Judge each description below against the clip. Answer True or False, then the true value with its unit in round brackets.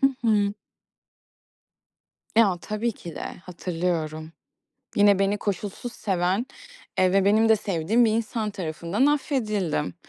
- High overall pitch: True (200 Hz)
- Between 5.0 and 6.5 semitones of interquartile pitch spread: False (3.8 semitones)